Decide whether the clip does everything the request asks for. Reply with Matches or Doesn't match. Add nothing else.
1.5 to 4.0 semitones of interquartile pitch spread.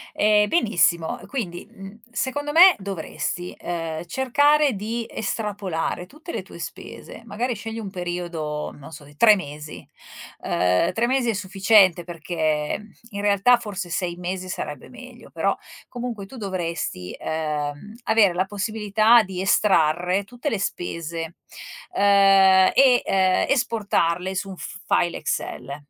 Doesn't match